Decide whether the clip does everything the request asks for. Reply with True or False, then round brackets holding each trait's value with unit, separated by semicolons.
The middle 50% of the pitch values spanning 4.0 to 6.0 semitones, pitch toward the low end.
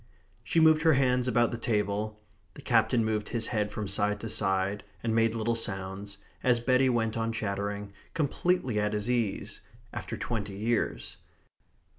False (2.7 semitones; 110 Hz)